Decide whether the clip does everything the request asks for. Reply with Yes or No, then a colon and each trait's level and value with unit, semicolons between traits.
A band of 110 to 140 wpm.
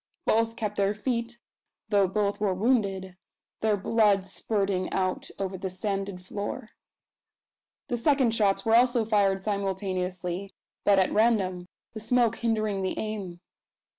Yes: slow, 135 wpm